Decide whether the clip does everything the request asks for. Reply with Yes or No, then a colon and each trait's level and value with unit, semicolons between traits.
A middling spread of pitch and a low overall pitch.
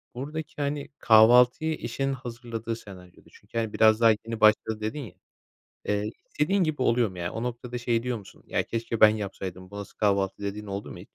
Yes: average, 3.0 semitones; low, 115 Hz